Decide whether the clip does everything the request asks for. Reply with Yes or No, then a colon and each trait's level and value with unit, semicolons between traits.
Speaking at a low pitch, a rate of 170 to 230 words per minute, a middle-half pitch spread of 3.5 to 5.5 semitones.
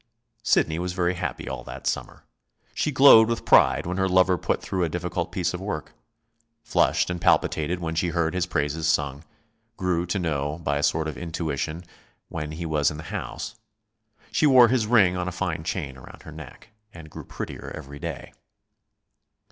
No: very low, 85 Hz; average, 185 wpm; average, 3.0 semitones